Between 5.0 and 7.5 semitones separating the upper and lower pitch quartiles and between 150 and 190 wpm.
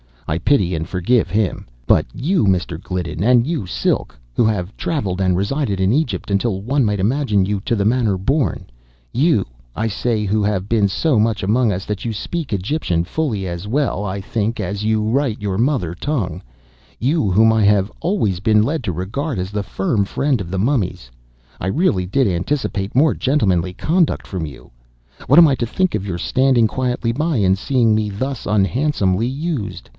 Yes: wide, 5.6 semitones; average, 180 wpm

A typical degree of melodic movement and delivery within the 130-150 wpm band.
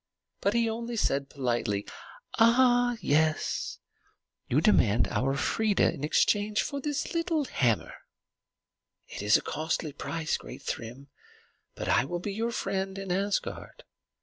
No: wide, 8.8 semitones; slow, 135 wpm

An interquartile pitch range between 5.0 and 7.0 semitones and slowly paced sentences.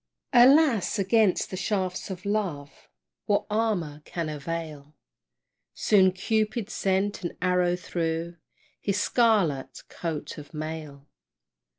No: average, 4.5 semitones; slow, 105 wpm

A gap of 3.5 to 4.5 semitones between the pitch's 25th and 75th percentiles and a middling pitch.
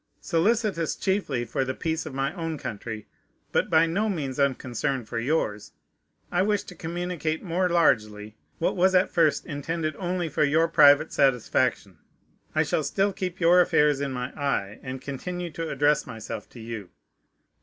No: average, 5.1 semitones; medium, 150 Hz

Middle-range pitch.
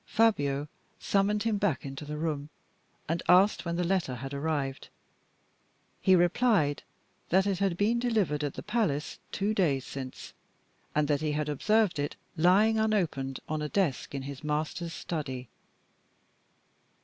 Yes: medium, 160 Hz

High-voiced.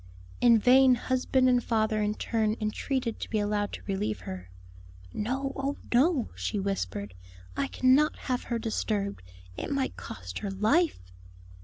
Yes: high, 225 Hz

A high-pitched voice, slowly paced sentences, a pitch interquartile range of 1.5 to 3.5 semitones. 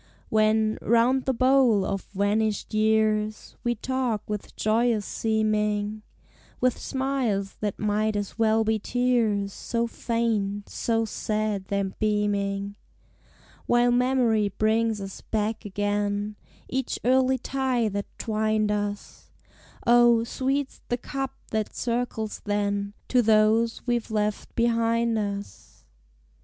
Yes: high, 220 Hz; slow, 115 wpm; narrow, 2.4 semitones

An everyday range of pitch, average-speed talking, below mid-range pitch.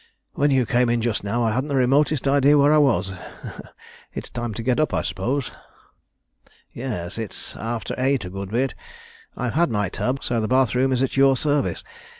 Yes: average, 3.3 semitones; average, 195 wpm; low, 125 Hz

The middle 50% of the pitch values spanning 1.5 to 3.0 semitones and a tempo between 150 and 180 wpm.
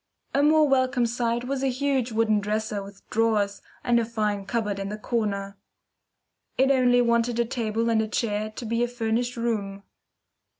Yes: narrow, 2.6 semitones; average, 175 wpm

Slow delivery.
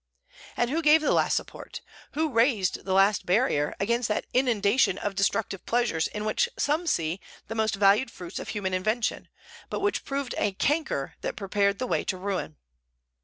No: average, 175 wpm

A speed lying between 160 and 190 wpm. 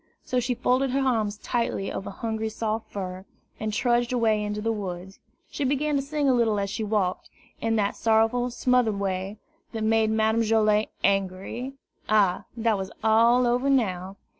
Yes: average, 170 wpm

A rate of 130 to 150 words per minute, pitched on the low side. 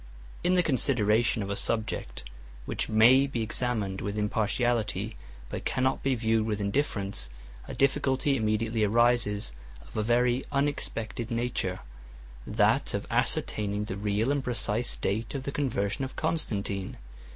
Yes: average, 140 wpm; low, 115 Hz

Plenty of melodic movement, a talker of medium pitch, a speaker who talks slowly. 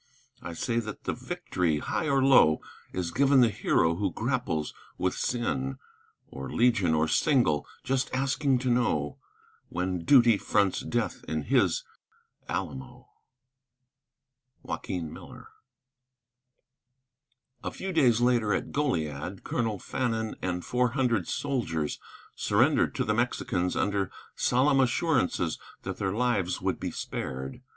No: wide, 6.9 semitones; low, 110 Hz; slow, 125 wpm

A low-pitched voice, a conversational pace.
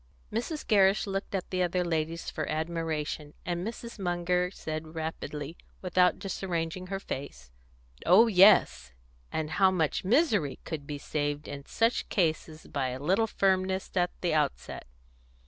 No: medium, 175 Hz; average, 145 wpm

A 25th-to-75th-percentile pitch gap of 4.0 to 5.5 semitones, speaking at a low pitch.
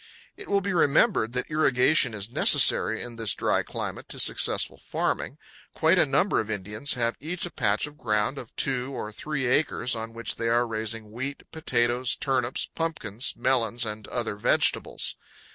Yes: average, 4.3 semitones; low, 120 Hz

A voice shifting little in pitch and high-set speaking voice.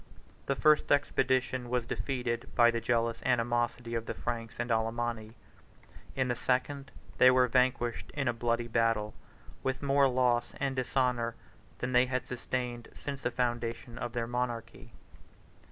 No: narrow, 1.6 semitones; low, 120 Hz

